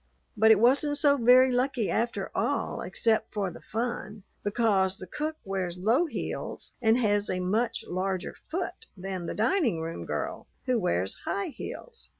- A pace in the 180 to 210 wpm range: No, average, 160 wpm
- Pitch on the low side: No, high, 220 Hz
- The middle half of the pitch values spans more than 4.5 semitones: Yes, average, 4.9 semitones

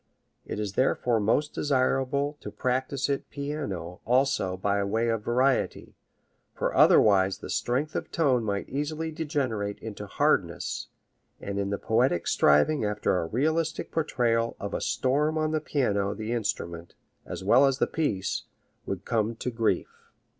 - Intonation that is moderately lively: No, wide, 5.7 semitones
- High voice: No, low, 120 Hz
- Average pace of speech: Yes, average, 150 wpm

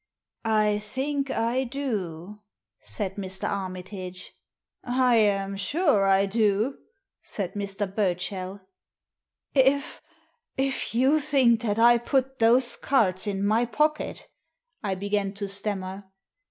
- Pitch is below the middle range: No, high, 210 Hz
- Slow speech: Yes, slow, 120 wpm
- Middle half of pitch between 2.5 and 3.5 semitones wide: No, average, 4.4 semitones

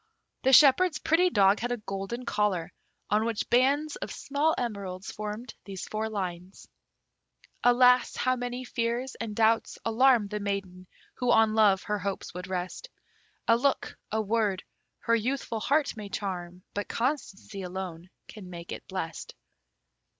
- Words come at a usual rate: Yes, average, 150 wpm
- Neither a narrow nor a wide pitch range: Yes, average, 4.3 semitones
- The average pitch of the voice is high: Yes, high, 215 Hz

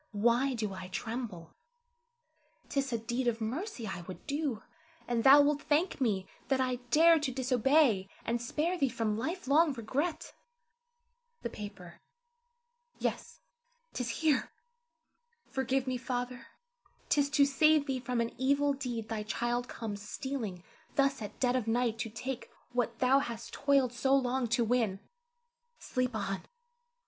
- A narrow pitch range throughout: No, average, 3.5 semitones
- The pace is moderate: Yes, average, 150 wpm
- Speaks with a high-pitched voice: Yes, very high, 250 Hz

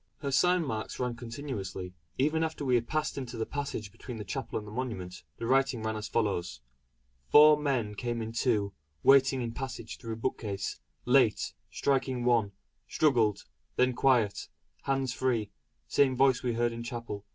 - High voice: No, low, 120 Hz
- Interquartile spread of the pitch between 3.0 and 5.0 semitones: Yes, average, 3.5 semitones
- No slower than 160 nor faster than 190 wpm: Yes, average, 165 wpm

